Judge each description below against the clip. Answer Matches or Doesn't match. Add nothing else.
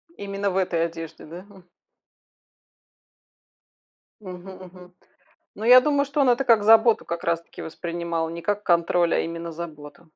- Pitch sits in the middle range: Matches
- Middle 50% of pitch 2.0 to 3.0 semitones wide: Doesn't match